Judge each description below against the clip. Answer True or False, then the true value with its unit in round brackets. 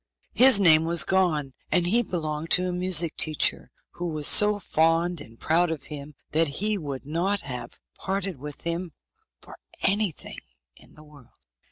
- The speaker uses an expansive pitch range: False (3.6 semitones)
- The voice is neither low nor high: True (165 Hz)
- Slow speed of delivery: False (165 wpm)